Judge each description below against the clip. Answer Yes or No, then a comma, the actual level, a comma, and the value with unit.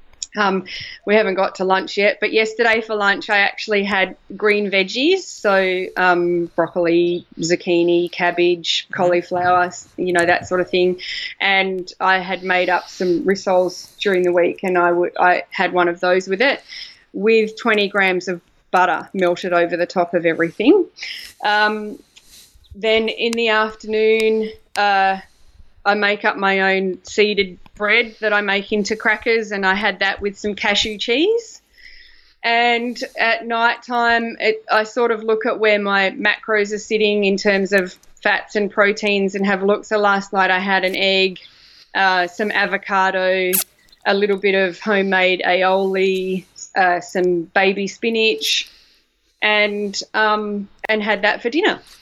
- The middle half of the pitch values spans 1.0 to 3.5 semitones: Yes, average, 2.8 semitones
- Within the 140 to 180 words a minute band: Yes, average, 155 wpm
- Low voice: No, high, 200 Hz